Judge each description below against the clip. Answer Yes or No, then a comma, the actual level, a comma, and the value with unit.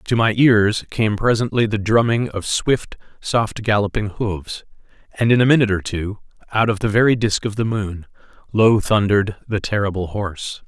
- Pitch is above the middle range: No, low, 105 Hz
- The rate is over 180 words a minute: No, average, 175 wpm